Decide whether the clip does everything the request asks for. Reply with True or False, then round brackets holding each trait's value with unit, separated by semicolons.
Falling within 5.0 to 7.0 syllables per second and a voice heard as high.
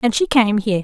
True (6.9 syllables/s; 220 Hz)